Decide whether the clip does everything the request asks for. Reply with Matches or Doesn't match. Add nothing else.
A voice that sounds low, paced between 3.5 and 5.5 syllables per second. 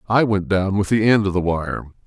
Matches